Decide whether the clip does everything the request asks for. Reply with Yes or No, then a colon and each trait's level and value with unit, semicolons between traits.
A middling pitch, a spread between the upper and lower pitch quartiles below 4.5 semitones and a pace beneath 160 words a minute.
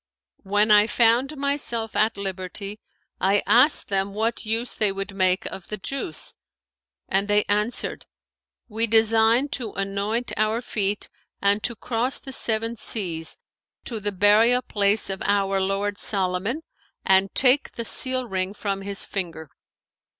No: high, 210 Hz; average, 2.7 semitones; average, 145 wpm